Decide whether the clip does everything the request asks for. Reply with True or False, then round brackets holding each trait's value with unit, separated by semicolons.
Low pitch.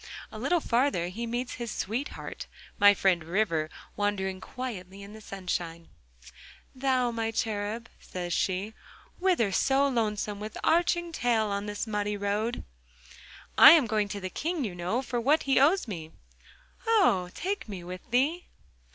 False (215 Hz)